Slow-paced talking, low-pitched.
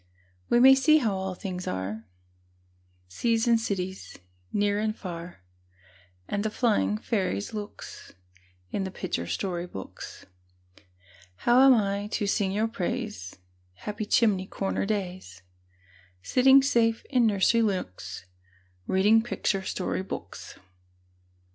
No: slow, 120 wpm; high, 205 Hz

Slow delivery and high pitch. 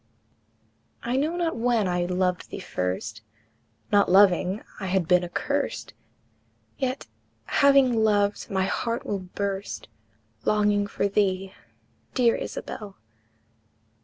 Yes: slow, 110 wpm; high, 200 Hz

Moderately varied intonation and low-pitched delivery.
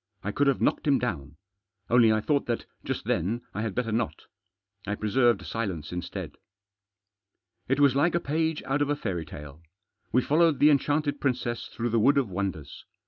No: wide, 5.8 semitones; low, 120 Hz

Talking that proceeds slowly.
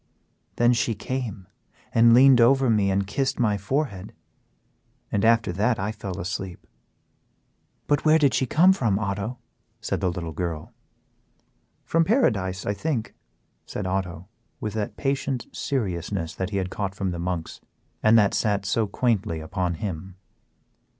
No: average, 150 wpm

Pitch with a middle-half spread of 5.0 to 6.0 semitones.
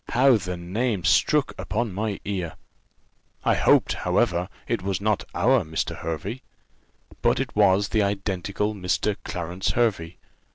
No: average, 3.3 semitones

